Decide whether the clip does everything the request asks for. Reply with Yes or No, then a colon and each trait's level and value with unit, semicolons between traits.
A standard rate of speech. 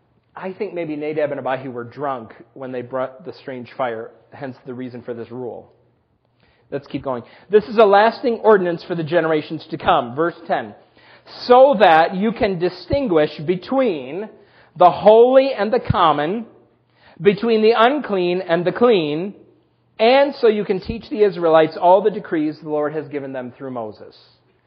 Yes: average, 170 wpm